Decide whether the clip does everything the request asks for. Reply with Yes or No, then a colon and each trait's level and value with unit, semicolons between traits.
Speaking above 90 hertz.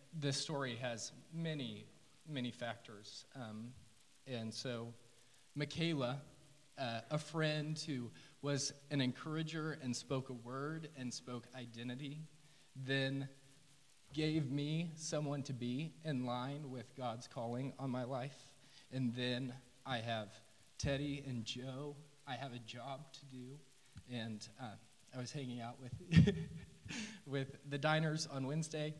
Yes: low, 135 Hz